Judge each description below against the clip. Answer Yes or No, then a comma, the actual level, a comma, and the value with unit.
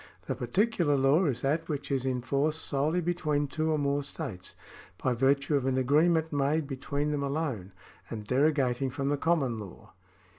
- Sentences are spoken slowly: No, average, 180 wpm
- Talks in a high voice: No, medium, 140 Hz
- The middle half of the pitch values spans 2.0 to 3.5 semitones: Yes, average, 2.9 semitones